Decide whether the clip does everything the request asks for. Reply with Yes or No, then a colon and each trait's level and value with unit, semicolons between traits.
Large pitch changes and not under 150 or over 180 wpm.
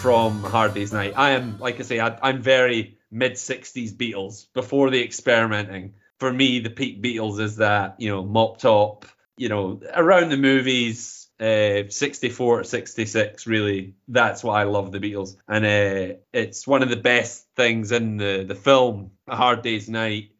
No: average, 3.4 semitones; average, 175 wpm